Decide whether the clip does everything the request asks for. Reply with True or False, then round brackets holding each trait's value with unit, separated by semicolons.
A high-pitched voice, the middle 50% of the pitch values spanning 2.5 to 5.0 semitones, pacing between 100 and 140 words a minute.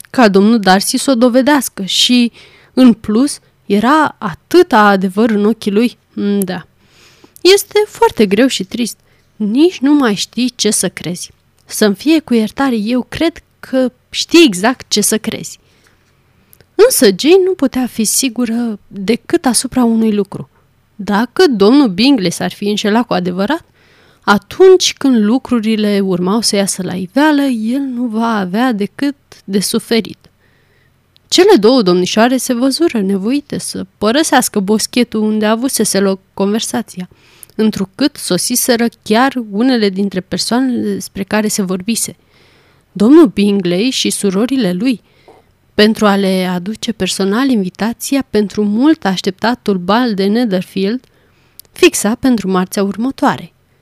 True (220 Hz; 4.5 semitones; 130 wpm)